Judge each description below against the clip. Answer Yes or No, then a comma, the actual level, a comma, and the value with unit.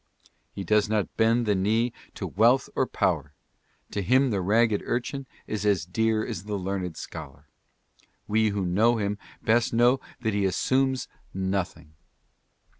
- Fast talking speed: No, average, 150 wpm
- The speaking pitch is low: Yes, low, 105 Hz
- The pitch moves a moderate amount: Yes, average, 3.4 semitones